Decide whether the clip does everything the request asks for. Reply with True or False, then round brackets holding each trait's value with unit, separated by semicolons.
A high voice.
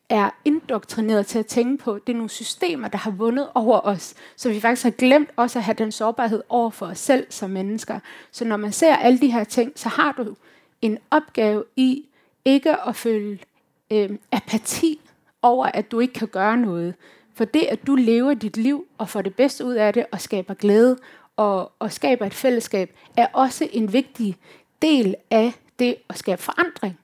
True (230 Hz)